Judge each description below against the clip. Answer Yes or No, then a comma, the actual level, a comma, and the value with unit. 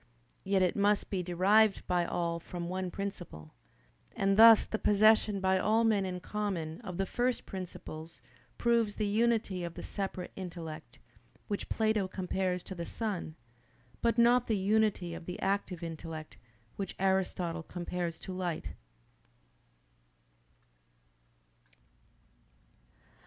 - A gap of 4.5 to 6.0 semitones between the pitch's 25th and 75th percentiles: No, average, 3.2 semitones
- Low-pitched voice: No, high, 190 Hz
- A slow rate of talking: Yes, slow, 125 wpm